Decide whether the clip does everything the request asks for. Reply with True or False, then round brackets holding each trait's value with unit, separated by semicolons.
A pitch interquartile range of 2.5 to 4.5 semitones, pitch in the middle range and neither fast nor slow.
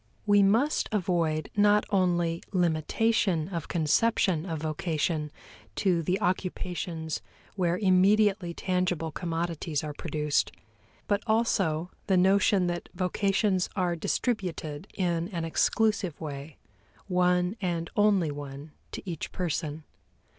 False (3.3 semitones; 180 Hz; 110 wpm)